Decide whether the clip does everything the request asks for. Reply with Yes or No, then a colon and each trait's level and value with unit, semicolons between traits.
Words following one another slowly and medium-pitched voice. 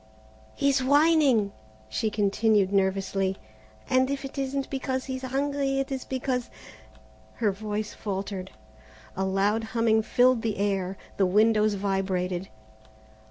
No: slow, 125 wpm; high, 220 Hz